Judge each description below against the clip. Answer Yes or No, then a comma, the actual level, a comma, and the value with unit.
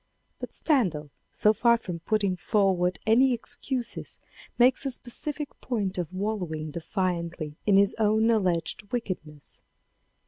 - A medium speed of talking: No, slow, 125 wpm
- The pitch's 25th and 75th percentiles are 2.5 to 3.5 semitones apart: No, average, 5.0 semitones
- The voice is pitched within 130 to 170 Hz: No, high, 200 Hz